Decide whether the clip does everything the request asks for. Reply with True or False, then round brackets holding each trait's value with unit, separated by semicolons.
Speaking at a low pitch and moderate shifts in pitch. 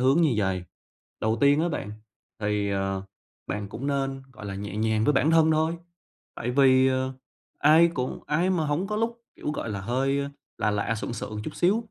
False (130 Hz; 6.6 semitones)